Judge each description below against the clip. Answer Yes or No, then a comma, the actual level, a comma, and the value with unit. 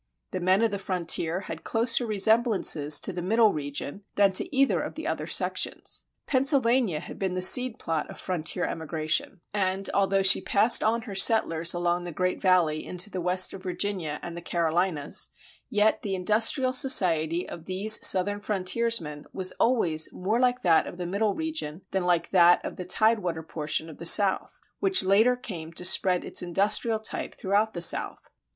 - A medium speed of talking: Yes, average, 180 wpm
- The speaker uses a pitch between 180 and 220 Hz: Yes, high, 190 Hz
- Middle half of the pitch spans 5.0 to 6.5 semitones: No, average, 4.1 semitones